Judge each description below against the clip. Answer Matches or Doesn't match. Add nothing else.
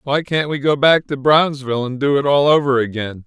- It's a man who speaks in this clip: Matches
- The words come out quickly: Matches